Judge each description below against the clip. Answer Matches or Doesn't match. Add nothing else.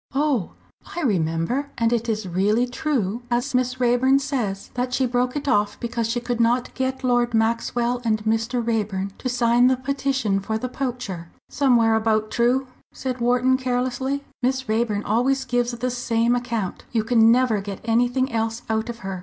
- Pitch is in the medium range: Doesn't match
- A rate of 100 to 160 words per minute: Doesn't match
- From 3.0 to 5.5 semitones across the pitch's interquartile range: Doesn't match